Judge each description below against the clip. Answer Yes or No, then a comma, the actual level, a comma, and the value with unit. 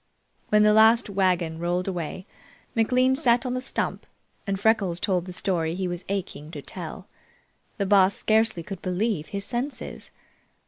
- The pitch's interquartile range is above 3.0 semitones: Yes, average, 3.8 semitones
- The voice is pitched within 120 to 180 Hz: No, high, 195 Hz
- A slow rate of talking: No, average, 155 wpm